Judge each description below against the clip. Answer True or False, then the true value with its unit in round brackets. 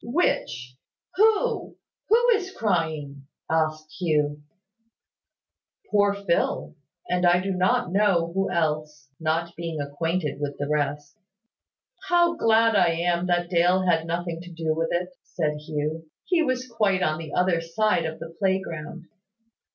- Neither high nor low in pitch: True (170 Hz)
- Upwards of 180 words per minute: False (140 wpm)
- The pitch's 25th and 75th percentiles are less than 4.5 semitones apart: True (3.8 semitones)